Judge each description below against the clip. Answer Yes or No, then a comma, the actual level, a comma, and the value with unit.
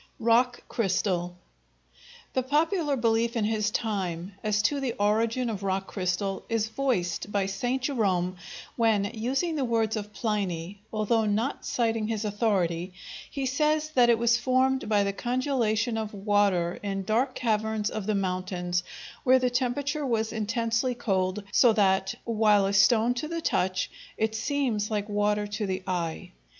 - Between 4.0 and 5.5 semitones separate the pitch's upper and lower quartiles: No, average, 3.6 semitones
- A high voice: Yes, high, 215 Hz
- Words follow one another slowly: No, average, 155 wpm